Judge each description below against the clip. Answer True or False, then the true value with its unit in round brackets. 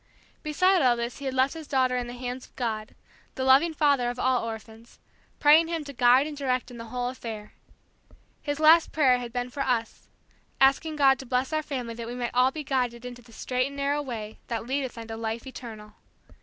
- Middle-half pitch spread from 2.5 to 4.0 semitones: True (2.8 semitones)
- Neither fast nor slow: False (215 wpm)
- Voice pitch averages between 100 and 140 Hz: False (255 Hz)